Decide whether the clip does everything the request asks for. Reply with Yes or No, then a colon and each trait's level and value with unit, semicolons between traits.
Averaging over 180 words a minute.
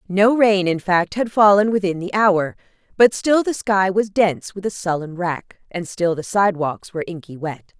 Yes: average, 200 wpm